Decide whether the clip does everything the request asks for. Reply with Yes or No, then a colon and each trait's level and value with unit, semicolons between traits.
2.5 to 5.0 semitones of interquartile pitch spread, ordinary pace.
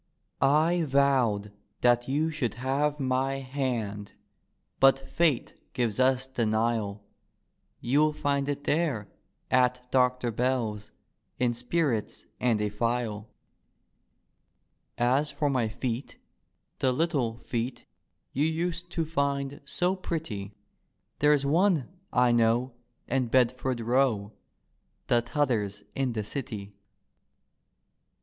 No: average, 3.4 semitones; slow, 110 wpm